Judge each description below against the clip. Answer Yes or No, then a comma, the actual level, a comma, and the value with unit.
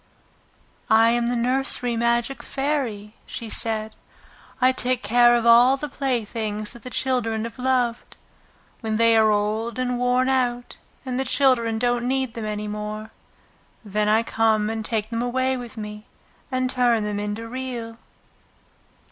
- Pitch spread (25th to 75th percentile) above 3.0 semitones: No, narrow, 2.4 semitones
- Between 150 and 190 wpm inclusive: Yes, average, 155 wpm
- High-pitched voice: Yes, high, 235 Hz